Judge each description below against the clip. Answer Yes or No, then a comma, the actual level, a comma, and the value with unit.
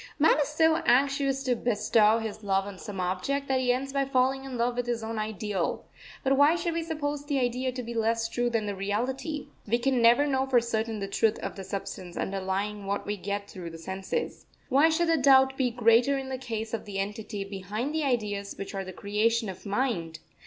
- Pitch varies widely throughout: No, average, 4.8 semitones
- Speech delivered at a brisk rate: Yes, fast, 220 wpm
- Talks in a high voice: Yes, high, 230 Hz